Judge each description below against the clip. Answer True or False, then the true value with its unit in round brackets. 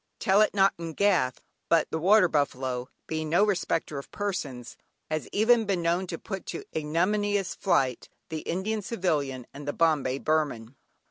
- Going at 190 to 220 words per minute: False (160 wpm)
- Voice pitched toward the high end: False (165 Hz)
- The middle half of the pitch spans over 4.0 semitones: True (5.4 semitones)